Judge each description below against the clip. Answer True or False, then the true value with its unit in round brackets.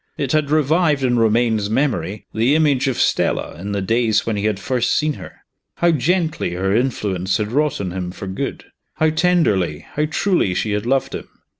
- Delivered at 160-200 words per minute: True (190 wpm)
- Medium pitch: False (120 Hz)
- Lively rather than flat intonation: True (7.0 semitones)